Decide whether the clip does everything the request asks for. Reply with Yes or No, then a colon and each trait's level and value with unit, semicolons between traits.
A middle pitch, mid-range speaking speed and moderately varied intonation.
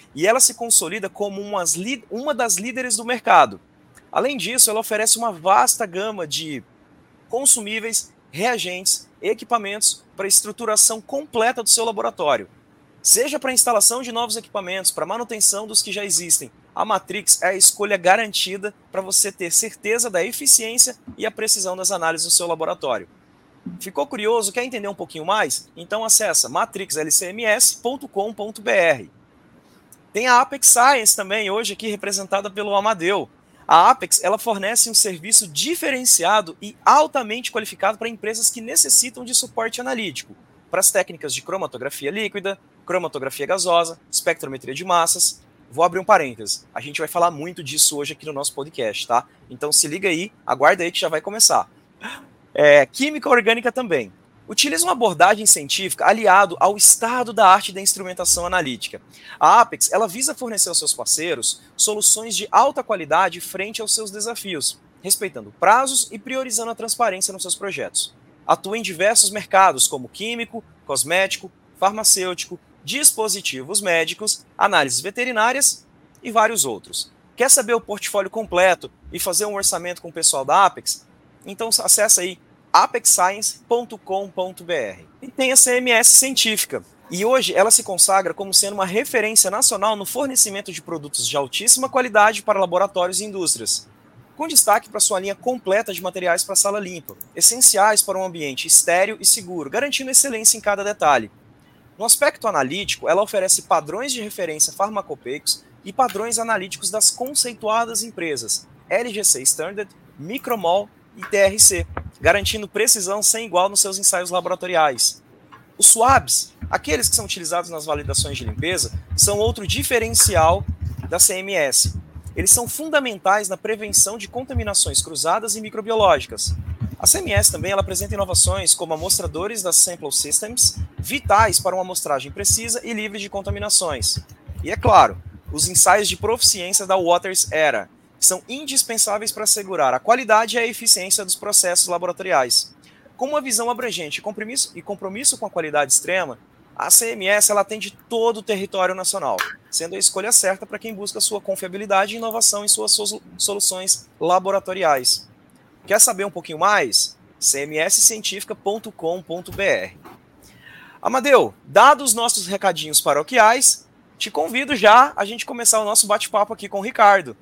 No: high, 205 Hz; average, 150 wpm; average, 4.1 semitones